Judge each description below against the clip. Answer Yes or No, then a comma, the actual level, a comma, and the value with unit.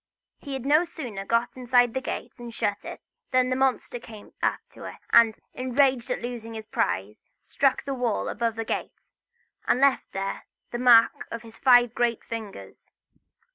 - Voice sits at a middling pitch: No, high, 240 Hz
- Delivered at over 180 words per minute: No, average, 175 wpm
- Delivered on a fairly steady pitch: Yes, narrow, 2.3 semitones